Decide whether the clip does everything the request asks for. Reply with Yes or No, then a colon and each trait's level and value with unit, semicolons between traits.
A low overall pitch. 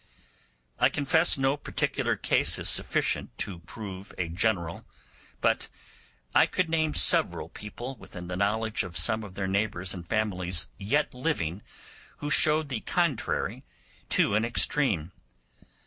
Yes: low, 105 Hz